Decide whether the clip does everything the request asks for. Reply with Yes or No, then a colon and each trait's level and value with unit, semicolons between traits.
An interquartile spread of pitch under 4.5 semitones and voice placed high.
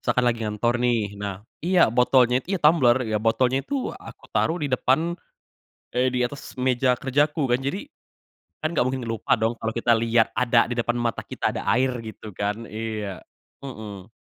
No: average, 2.7 semitones; low, 120 Hz